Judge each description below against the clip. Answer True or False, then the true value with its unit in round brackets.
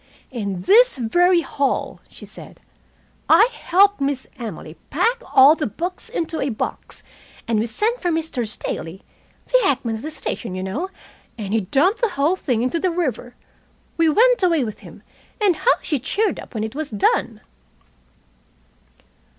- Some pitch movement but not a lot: False (8.0 semitones)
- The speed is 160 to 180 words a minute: True (165 wpm)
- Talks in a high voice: True (285 Hz)